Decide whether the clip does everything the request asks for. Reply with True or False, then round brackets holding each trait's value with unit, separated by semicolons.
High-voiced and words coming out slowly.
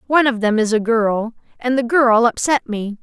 False (235 Hz; 220 wpm)